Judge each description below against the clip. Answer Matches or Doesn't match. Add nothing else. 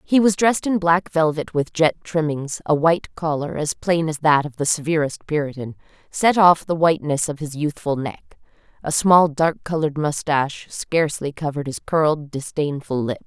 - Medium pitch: Matches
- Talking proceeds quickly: Doesn't match